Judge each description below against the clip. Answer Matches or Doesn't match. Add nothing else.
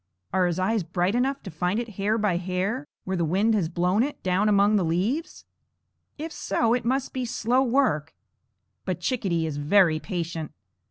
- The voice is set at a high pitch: Matches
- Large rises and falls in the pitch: Doesn't match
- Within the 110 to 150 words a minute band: Doesn't match